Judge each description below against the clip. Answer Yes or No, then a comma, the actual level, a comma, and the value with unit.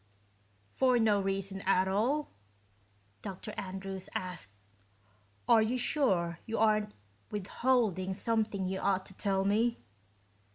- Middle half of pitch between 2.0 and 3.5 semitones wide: Yes, average, 2.8 semitones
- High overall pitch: Yes, high, 200 Hz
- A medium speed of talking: No, slow, 115 wpm